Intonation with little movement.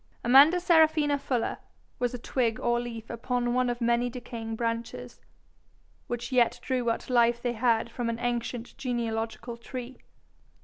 Yes: narrow, 1.4 semitones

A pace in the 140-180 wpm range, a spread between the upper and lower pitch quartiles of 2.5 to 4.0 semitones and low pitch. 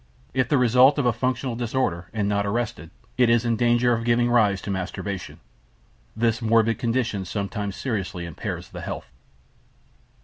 Yes: average, 160 wpm; average, 3.2 semitones; low, 115 Hz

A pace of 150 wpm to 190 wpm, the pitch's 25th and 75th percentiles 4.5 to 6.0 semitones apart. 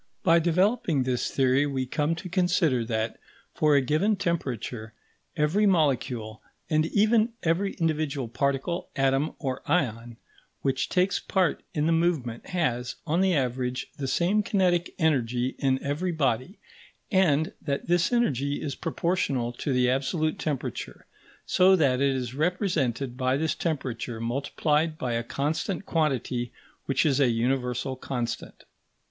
No: average, 140 wpm; average, 5.0 semitones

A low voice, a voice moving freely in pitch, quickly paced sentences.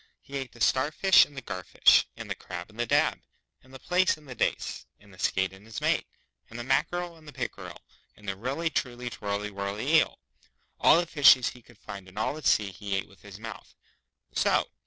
Yes: low, 115 Hz; wide, 5.7 semitones; fast, 220 wpm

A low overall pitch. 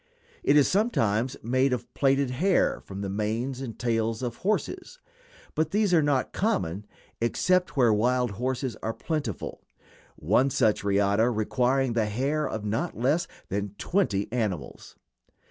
Yes: low, 125 Hz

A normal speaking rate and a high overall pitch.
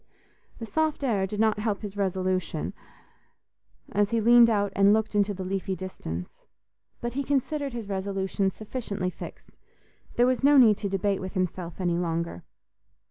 Yes: average, 160 wpm; high, 200 Hz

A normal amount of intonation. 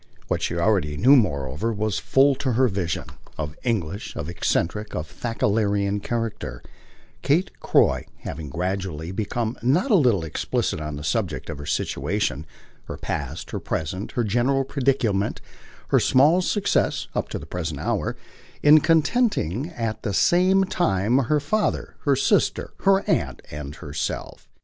No: wide, 8.3 semitones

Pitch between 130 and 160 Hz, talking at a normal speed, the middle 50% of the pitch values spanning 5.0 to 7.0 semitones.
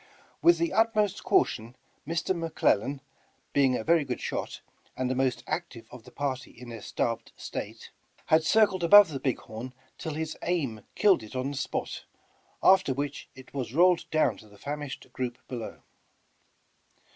Yes: medium, 140 Hz; average, 170 wpm; average, 5.3 semitones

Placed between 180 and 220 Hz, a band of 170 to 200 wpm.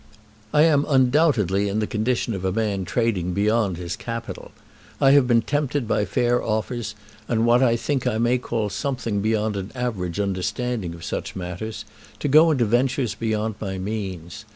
No: low, 110 Hz; average, 175 wpm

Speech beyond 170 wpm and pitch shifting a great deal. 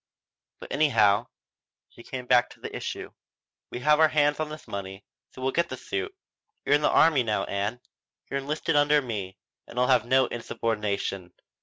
Yes: average, 180 wpm; wide, 5.9 semitones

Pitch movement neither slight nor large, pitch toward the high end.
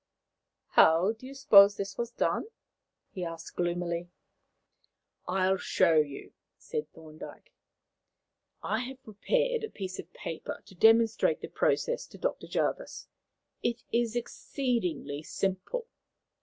No: wide, 6.1 semitones; high, 200 Hz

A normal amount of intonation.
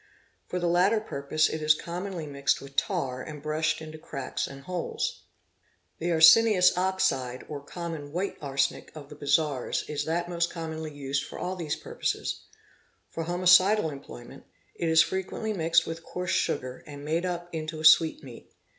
Yes: average, 3.4 semitones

